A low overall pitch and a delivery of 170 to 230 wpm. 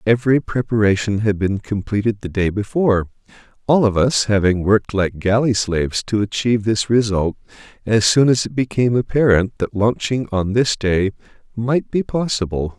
No: low, 110 Hz; average, 160 wpm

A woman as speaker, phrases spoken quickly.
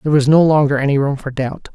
No: male; fast, 275 wpm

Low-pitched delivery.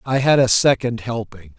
Yes: low, 120 Hz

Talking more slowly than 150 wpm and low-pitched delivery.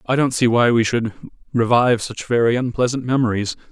No: average, 175 wpm; low, 120 Hz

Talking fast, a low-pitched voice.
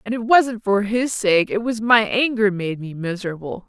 No: fast, 210 wpm; high, 210 Hz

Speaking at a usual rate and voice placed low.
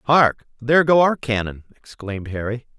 Yes: average, 150 wpm; low, 120 Hz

